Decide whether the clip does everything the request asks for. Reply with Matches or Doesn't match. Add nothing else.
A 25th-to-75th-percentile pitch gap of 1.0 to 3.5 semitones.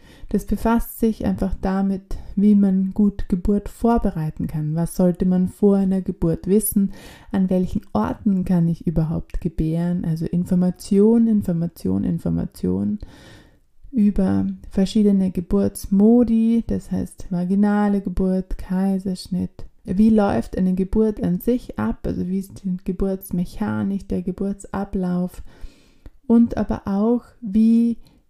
Matches